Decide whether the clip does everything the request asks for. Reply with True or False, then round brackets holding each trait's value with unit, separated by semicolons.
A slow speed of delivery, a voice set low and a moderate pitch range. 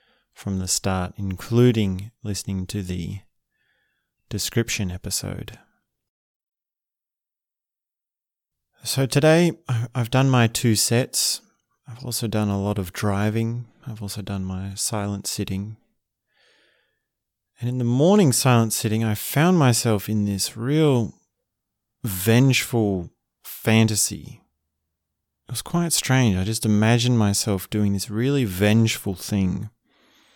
True (110 wpm; 110 Hz; 3.5 semitones)